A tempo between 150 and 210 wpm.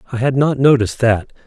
Yes: fast, 205 wpm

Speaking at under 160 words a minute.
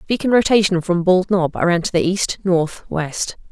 No: fast, 205 wpm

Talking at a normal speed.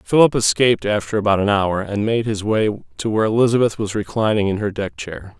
No: fast, 210 wpm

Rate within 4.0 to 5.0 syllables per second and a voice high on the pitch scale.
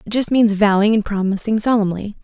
No: 5.8 syllables/s; high, 210 Hz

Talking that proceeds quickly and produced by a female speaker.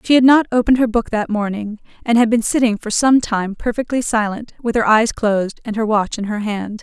Yes: fast, 235 wpm; female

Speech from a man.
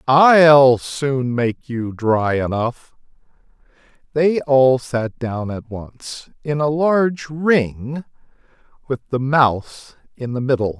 Yes: male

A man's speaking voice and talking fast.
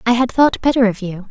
No: female; fast, 275 wpm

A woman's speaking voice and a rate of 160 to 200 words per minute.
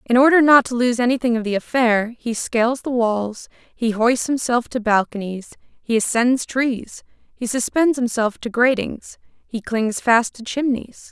Yes: female; average, 165 wpm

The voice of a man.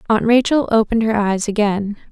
No: female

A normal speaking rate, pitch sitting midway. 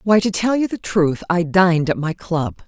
No: fast, 245 wpm; medium, 175 Hz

